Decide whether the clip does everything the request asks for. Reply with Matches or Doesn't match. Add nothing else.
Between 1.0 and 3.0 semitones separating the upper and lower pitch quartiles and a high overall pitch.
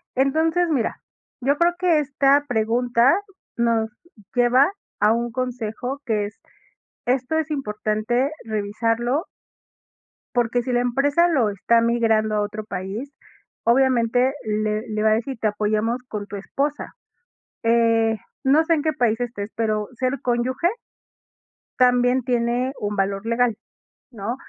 Doesn't match